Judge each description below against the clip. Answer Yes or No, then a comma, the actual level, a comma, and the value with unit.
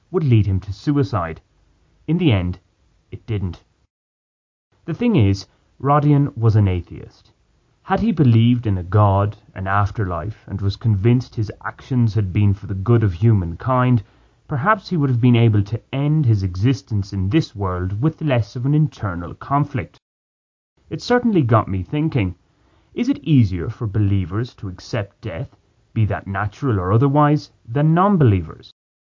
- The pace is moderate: Yes, average, 160 wpm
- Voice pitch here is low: Yes, low, 110 Hz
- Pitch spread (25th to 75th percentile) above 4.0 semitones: Yes, wide, 5.4 semitones